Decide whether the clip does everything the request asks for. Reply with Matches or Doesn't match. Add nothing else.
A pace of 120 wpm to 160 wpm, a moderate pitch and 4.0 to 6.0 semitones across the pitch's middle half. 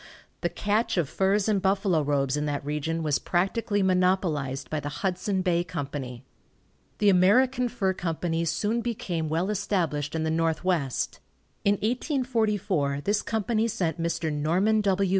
Matches